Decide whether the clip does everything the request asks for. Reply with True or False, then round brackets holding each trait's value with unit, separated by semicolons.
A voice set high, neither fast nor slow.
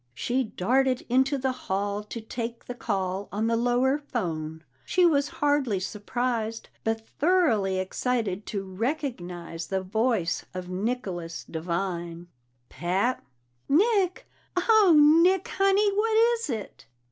False (230 Hz; 125 wpm)